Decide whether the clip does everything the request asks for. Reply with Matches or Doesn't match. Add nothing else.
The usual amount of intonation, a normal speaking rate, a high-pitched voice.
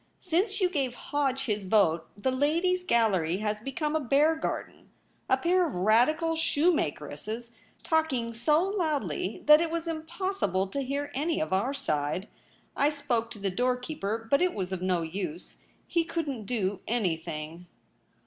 Doesn't match